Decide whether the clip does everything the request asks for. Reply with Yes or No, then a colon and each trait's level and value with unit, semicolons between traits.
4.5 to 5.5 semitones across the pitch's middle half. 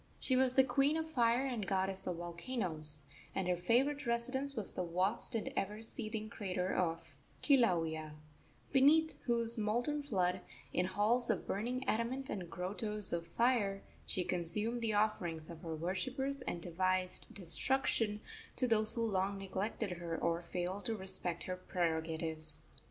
Yes: average, 5.1 semitones